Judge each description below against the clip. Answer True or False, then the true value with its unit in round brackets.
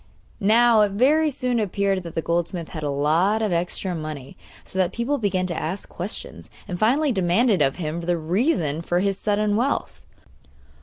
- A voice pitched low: False (190 Hz)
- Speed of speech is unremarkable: True (175 wpm)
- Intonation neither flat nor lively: True (4.6 semitones)